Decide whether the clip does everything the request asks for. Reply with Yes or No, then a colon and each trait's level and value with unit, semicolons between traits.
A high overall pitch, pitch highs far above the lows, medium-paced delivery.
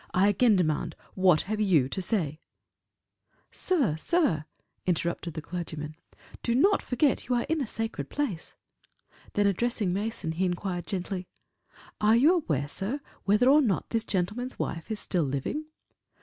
Yes: high, 195 Hz; wide, 5.9 semitones; average, 150 wpm